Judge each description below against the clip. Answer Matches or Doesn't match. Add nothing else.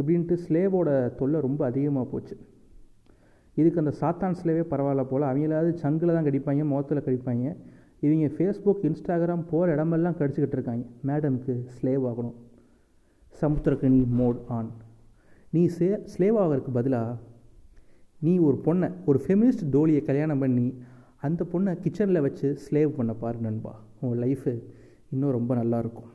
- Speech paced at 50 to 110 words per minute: Doesn't match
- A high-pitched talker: Doesn't match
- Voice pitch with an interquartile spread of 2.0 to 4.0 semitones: Doesn't match